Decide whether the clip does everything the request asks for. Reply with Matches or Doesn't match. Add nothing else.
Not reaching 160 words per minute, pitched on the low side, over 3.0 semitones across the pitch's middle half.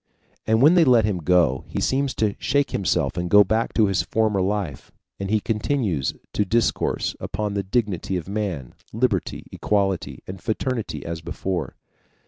Doesn't match